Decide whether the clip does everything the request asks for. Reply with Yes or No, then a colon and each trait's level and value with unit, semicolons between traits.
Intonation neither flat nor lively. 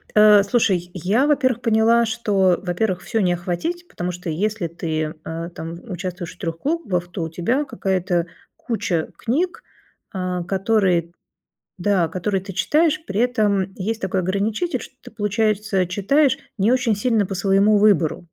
Yes: average, 4.0 semitones